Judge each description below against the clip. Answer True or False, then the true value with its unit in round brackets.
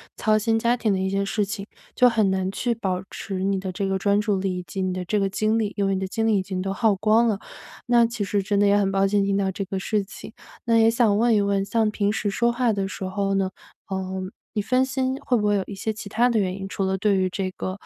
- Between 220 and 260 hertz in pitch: False (200 Hz)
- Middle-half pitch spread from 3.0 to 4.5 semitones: False (2.4 semitones)